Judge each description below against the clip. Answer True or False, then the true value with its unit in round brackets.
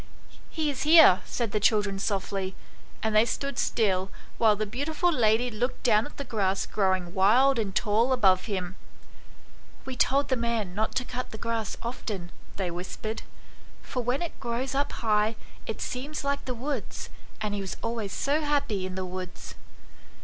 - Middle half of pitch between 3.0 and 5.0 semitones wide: True (4.6 semitones)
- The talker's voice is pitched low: False (220 Hz)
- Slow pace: False (175 wpm)